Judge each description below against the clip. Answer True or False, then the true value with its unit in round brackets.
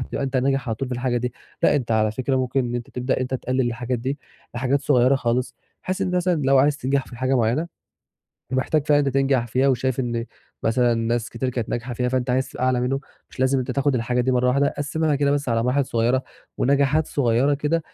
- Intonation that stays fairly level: True (2.2 semitones)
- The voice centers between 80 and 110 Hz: False (130 Hz)